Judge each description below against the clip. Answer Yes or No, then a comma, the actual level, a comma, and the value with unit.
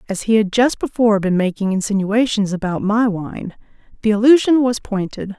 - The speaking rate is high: No, average, 165 wpm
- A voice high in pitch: Yes, high, 215 Hz